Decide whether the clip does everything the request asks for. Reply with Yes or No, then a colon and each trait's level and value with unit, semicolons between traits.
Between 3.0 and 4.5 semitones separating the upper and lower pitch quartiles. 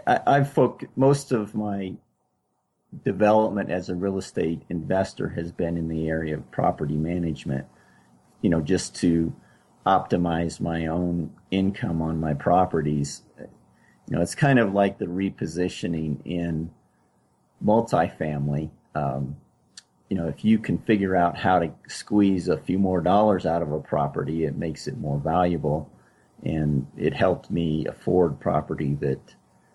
Yes: average, 4.0 semitones